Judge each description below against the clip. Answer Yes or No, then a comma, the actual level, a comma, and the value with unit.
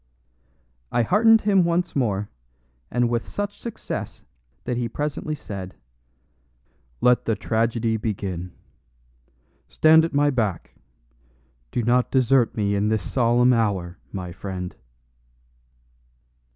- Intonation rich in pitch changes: Yes, wide, 5.8 semitones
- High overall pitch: No, low, 120 Hz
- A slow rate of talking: Yes, slow, 110 wpm